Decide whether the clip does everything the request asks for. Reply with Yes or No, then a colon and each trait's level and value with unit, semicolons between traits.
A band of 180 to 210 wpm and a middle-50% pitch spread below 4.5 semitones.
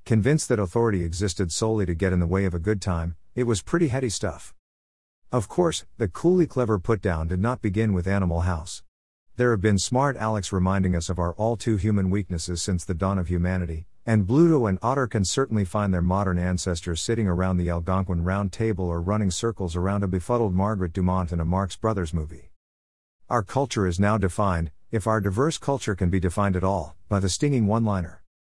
Yes: fast, 205 wpm; average, 3.7 semitones